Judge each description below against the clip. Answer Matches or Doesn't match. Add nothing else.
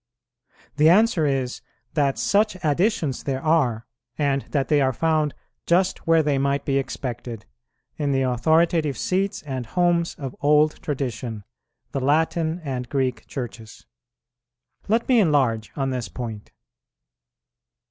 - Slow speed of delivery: Matches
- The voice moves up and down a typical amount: Matches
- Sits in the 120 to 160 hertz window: Matches